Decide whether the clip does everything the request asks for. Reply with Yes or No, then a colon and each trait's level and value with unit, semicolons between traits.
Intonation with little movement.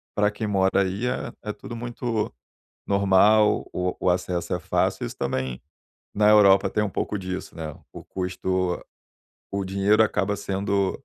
Yes: narrow, 2.2 semitones